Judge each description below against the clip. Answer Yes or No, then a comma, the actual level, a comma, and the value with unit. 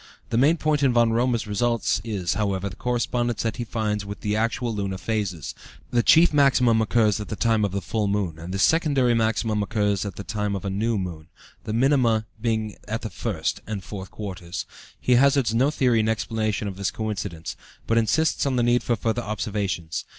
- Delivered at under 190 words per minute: No, average, 200 wpm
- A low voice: Yes, low, 110 Hz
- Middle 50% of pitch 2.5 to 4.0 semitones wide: Yes, average, 3.0 semitones